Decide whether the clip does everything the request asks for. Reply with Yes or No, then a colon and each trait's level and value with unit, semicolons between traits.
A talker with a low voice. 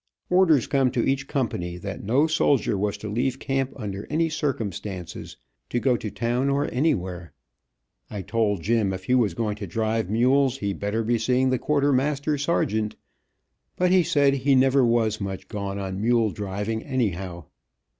Yes: low, 115 Hz